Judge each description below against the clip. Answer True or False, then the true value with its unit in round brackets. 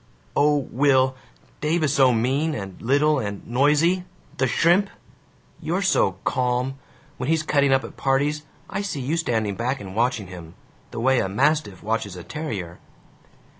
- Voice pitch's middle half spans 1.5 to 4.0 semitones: False (5.0 semitones)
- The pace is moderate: True (160 wpm)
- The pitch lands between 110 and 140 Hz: True (135 Hz)